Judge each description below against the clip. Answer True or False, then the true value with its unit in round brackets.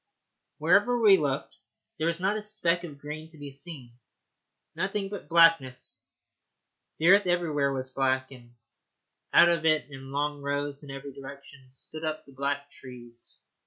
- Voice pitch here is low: False (145 Hz)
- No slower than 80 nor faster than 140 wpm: False (160 wpm)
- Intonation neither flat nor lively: True (3.7 semitones)